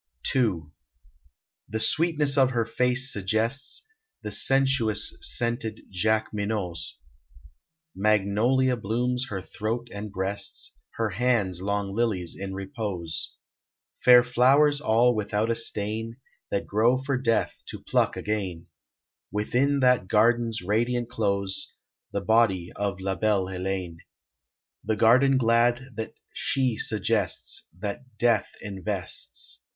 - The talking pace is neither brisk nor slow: No, slow, 115 wpm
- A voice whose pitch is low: Yes, low, 110 Hz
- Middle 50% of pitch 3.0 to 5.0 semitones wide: Yes, average, 3.7 semitones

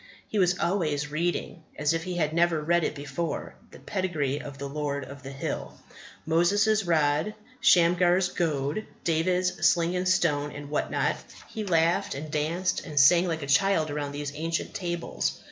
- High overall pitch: No, medium, 165 Hz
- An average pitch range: Yes, average, 3.4 semitones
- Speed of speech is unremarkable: Yes, average, 170 wpm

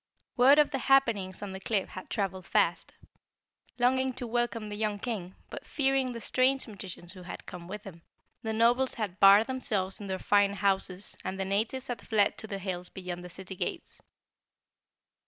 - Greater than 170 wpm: Yes, average, 185 wpm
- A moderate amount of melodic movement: Yes, average, 4.3 semitones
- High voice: Yes, high, 205 Hz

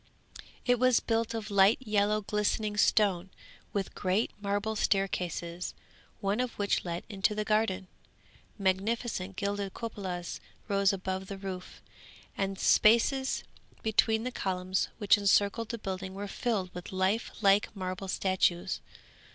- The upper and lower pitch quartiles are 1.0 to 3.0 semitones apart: Yes, narrow, 2.4 semitones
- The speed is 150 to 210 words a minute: No, slow, 135 wpm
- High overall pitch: Yes, high, 200 Hz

